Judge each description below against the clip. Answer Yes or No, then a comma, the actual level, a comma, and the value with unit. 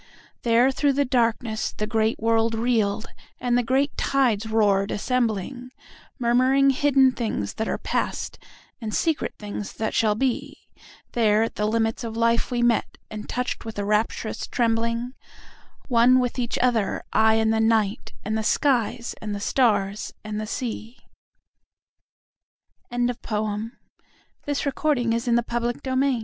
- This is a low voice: No, high, 230 Hz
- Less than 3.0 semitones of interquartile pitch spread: Yes, narrow, 2.4 semitones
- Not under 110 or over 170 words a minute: Yes, average, 140 wpm